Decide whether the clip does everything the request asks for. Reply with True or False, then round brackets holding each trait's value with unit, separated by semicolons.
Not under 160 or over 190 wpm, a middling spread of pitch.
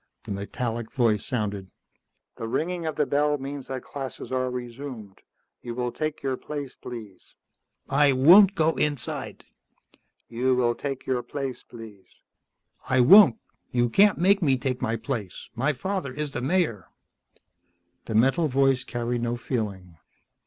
False (145 wpm; 3.7 semitones)